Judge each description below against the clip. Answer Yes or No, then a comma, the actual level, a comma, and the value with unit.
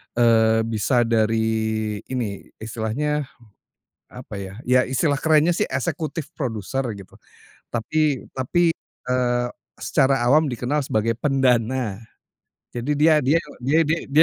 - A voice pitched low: Yes, low, 125 Hz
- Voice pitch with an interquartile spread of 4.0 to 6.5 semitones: Yes, average, 4.6 semitones